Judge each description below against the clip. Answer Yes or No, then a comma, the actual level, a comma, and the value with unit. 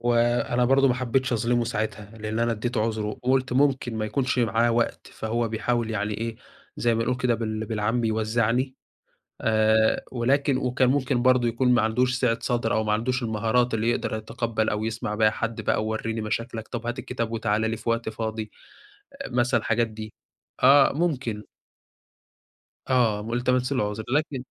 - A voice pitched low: Yes, low, 115 Hz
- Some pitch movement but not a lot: No, narrow, 2.2 semitones